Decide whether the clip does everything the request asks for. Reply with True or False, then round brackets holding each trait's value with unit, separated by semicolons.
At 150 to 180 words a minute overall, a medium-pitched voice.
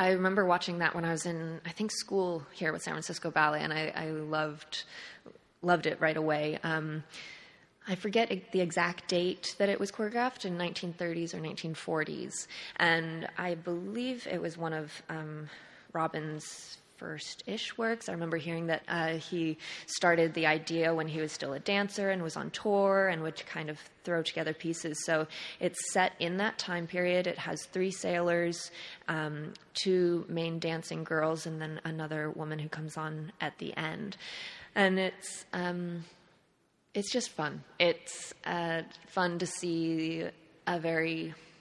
True (165 wpm; 170 Hz)